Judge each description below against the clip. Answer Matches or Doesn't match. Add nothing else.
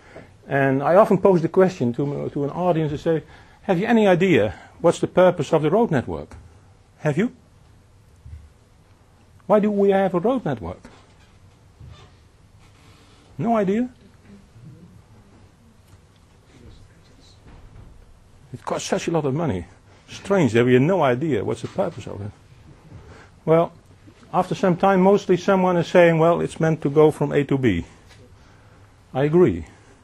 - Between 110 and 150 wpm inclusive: Matches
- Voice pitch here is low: Matches